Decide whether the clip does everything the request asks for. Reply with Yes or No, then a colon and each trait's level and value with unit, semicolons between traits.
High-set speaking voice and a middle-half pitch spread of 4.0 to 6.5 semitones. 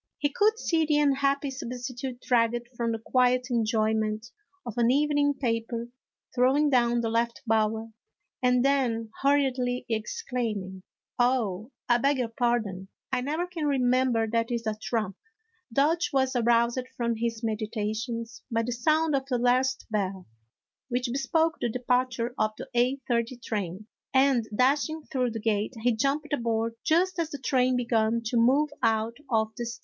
No: high, 245 Hz; average, 2.9 semitones